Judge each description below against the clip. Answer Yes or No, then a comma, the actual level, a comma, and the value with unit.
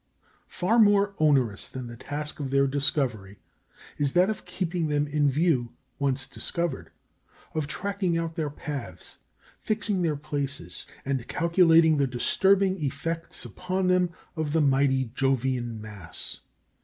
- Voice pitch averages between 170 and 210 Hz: No, medium, 150 Hz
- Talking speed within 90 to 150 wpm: Yes, slow, 135 wpm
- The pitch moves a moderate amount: Yes, average, 4.5 semitones